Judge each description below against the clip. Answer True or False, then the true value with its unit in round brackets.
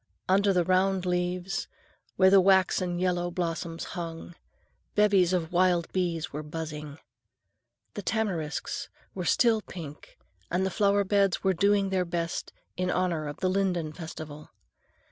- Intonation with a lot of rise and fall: False (2.5 semitones)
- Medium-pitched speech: True (180 Hz)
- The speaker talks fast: False (140 wpm)